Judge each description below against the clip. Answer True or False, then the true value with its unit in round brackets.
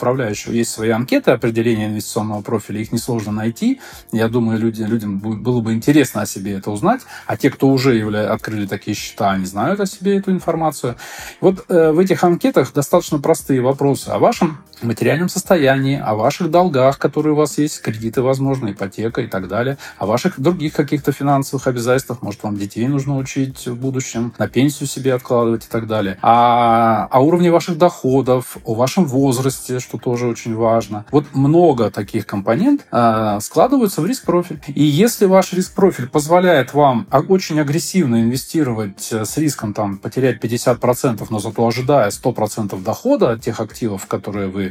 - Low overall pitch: True (125 Hz)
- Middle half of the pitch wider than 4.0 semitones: True (5.2 semitones)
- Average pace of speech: False (165 wpm)